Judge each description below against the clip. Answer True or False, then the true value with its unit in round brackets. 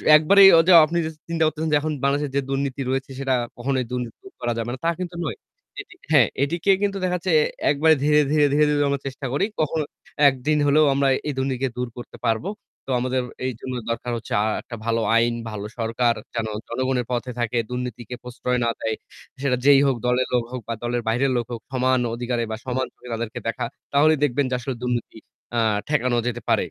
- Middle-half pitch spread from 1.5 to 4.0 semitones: True (3.5 semitones)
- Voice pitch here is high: False (130 Hz)